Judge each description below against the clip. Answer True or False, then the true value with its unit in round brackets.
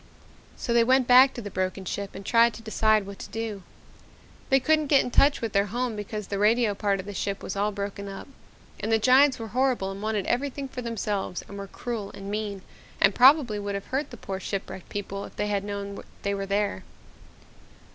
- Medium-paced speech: False (220 wpm)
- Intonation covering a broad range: False (3.4 semitones)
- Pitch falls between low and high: False (210 Hz)